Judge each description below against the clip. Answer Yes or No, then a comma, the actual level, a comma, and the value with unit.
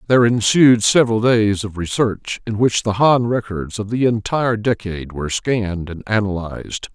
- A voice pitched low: Yes, low, 110 Hz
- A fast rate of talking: No, average, 165 wpm